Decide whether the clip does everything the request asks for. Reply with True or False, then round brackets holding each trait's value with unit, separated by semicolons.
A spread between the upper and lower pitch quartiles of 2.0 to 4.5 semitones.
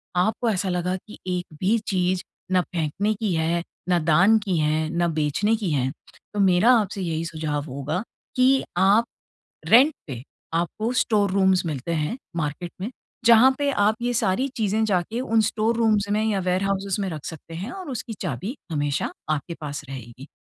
False (5.2 semitones)